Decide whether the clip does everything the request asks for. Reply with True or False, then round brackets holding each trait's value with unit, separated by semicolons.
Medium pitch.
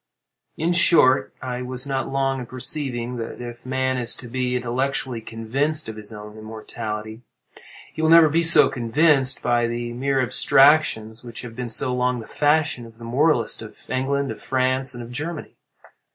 False (125 Hz)